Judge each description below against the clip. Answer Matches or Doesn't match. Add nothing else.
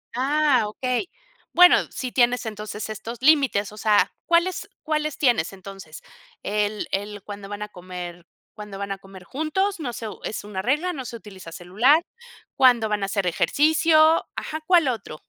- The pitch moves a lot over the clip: Matches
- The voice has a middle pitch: Doesn't match